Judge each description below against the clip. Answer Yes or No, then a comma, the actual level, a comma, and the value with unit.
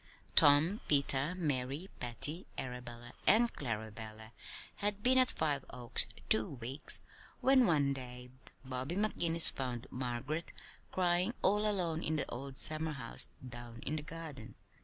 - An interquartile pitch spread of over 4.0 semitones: Yes, wide, 5.5 semitones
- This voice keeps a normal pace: No, slow, 130 wpm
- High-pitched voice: No, medium, 140 Hz